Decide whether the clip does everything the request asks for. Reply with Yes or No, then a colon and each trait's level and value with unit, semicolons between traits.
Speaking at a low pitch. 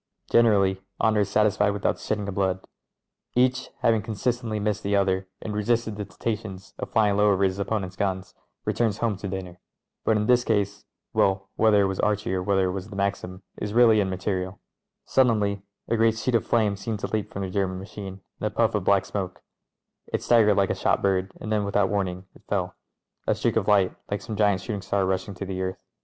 Yes: low, 100 Hz